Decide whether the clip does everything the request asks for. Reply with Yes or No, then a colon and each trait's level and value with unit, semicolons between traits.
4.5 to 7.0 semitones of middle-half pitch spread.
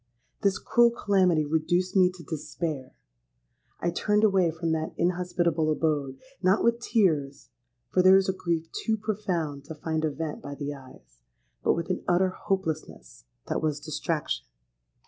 No: average, 4.0 semitones